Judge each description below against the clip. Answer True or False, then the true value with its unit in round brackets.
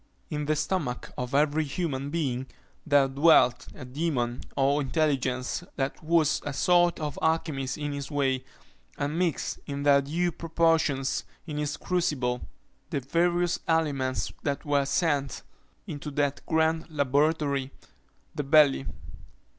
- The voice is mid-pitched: True (145 Hz)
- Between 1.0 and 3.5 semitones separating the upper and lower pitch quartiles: True (2.8 semitones)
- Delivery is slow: True (130 wpm)